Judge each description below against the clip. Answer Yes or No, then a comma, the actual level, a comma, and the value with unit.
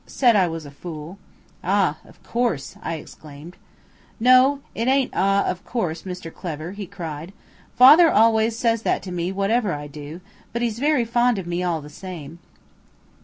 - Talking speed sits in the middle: Yes, average, 170 wpm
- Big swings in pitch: Yes, wide, 6.1 semitones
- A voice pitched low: No, high, 190 Hz